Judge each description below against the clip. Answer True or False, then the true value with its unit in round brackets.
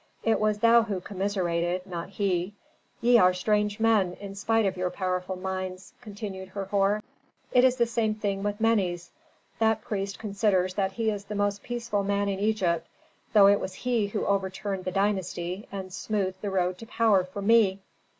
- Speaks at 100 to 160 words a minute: False (180 wpm)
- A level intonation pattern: True (2.3 semitones)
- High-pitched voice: True (200 Hz)